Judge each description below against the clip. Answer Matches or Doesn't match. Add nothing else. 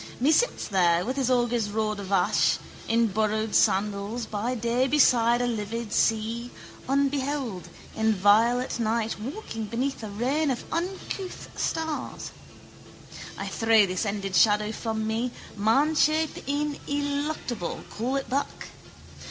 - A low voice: Doesn't match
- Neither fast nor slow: Doesn't match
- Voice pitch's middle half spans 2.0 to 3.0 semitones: Doesn't match